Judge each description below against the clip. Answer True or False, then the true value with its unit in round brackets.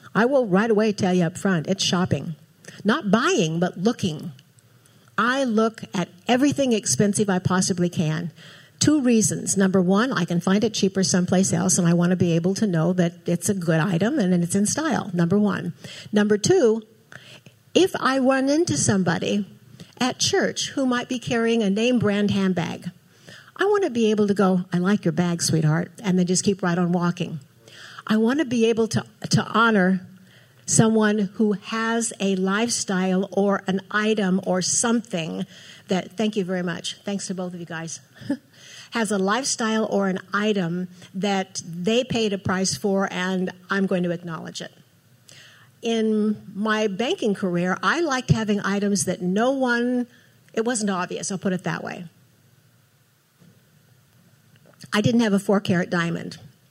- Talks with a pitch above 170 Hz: True (190 Hz)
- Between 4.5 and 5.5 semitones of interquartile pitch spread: False (3.8 semitones)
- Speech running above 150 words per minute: True (170 wpm)